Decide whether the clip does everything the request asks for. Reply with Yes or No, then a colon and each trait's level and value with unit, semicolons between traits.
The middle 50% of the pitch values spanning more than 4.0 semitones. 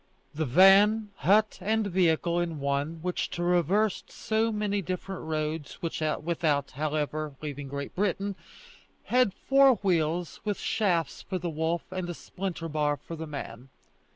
Yes: average, 4.4 semitones